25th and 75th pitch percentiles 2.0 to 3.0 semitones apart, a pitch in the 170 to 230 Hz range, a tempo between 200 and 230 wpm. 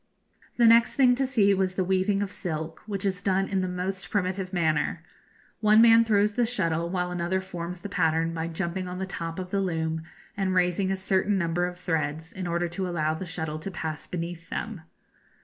Yes: average, 2.7 semitones; medium, 185 Hz; fast, 205 wpm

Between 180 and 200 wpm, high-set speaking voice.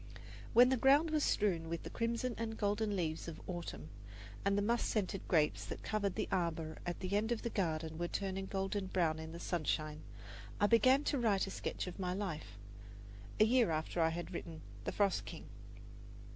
Yes: average, 195 wpm; high, 195 Hz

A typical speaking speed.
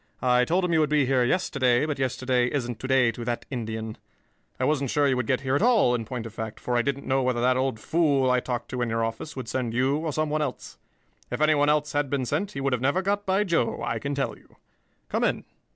No: fast, 265 wpm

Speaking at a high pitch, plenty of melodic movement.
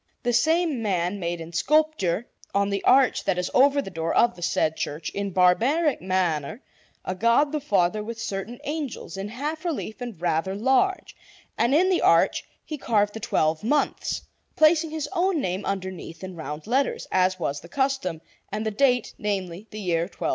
Yes: high, 210 Hz; wide, 7.3 semitones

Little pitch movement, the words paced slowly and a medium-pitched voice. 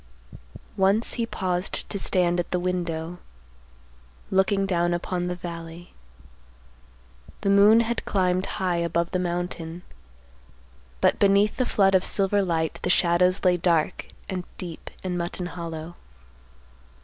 Yes: narrow, 2.0 semitones; slow, 130 wpm; medium, 180 Hz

